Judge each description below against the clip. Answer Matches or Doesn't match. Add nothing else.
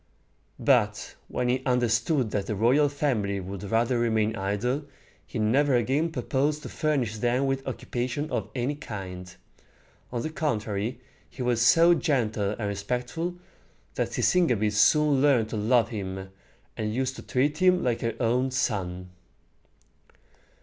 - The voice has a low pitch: Matches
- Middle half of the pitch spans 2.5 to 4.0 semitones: Doesn't match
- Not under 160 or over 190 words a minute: Doesn't match